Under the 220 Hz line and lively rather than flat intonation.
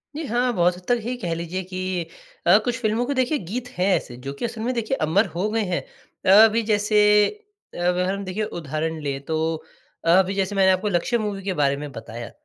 No: high, 190 Hz; average, 4.2 semitones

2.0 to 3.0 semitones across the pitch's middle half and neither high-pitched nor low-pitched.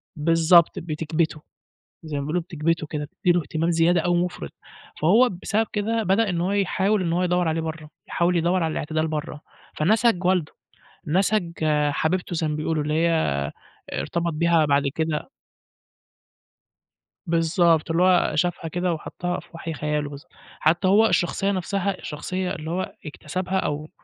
Yes: average, 2.7 semitones; medium, 170 Hz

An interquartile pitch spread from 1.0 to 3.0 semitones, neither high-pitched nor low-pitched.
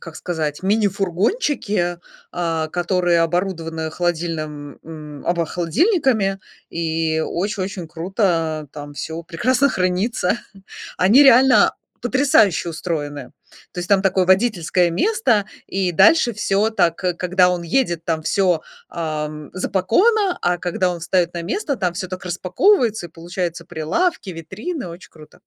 No: average, 3.9 semitones; medium, 180 Hz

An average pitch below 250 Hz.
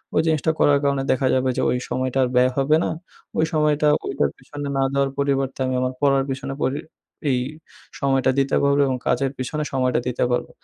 Yes: low, 135 Hz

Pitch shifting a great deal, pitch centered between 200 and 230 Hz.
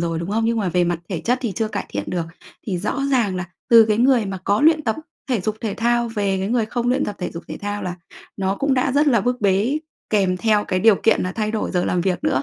No: average, 4.2 semitones; high, 210 Hz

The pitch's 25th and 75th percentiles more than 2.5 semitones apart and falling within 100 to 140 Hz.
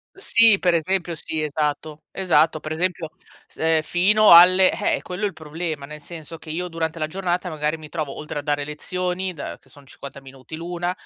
No: average, 2.9 semitones; medium, 160 Hz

